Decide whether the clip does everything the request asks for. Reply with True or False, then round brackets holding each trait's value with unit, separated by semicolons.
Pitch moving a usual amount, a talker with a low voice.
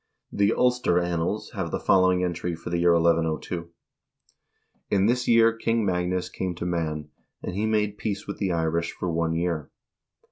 True (3.3 semitones; 90 Hz)